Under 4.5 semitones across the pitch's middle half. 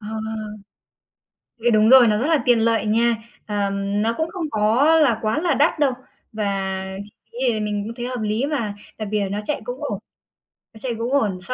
Yes: average, 3.7 semitones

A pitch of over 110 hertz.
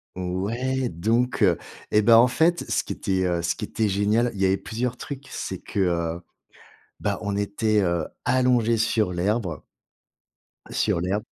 No: low, 105 Hz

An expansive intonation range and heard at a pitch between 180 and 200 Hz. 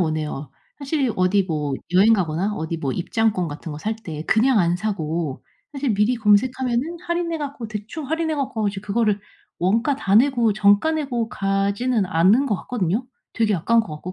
No: wide, 5.8 semitones; high, 210 Hz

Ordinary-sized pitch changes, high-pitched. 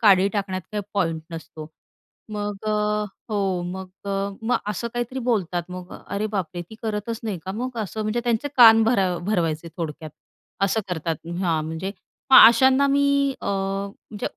Yes: average, 3.7 semitones; high, 200 Hz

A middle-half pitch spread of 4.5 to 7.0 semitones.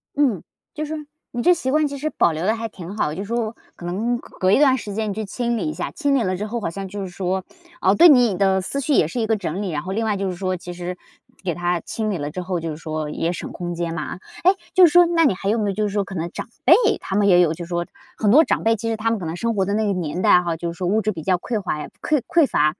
Yes: average, 4.8 semitones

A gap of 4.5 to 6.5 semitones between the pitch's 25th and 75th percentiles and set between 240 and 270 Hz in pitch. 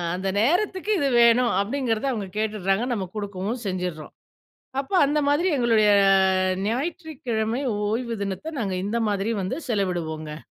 No: average, 5.0 semitones; high, 220 Hz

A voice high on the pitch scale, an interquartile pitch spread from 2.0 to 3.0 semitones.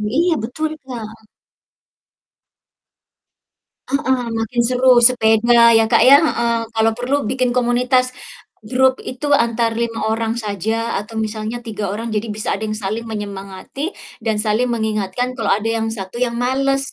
Yes: high, 230 Hz; narrow, 2.5 semitones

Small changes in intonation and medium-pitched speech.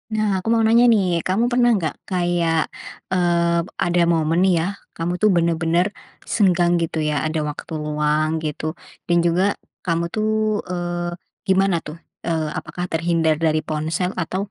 Yes: narrow, 2.2 semitones; medium, 175 Hz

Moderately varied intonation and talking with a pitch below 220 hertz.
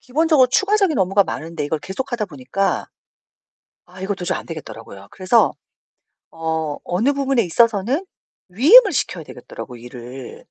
No: wide, 8.8 semitones; high, 190 Hz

